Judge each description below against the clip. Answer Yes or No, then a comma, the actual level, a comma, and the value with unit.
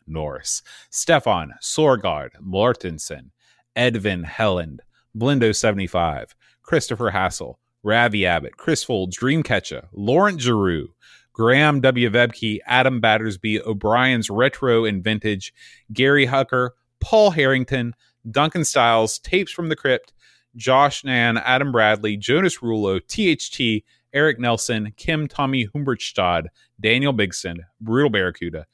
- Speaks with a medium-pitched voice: No, low, 115 Hz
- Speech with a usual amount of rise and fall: Yes, average, 3.9 semitones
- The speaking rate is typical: No, slow, 105 wpm